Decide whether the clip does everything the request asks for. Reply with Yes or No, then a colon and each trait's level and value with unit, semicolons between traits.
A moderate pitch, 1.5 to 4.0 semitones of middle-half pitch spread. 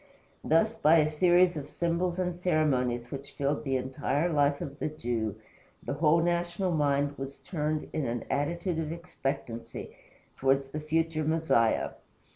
Yes: medium, 150 Hz; average, 3.6 semitones